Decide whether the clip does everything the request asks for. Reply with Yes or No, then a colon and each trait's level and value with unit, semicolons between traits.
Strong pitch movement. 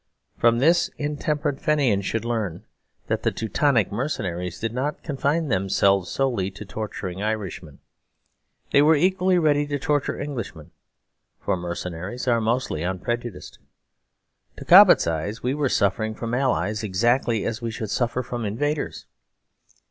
Yes: wide, 6.3 semitones